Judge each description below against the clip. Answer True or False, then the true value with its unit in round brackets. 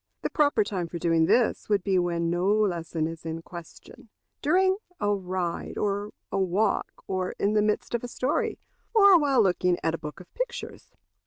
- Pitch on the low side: False (195 Hz)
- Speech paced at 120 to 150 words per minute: False (185 wpm)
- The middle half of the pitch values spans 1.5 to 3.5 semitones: False (4.4 semitones)